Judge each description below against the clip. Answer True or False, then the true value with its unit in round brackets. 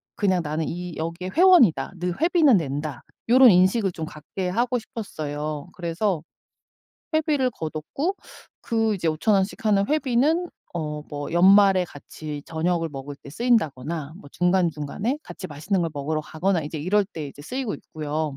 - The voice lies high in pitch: False (180 Hz)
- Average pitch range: False (6.1 semitones)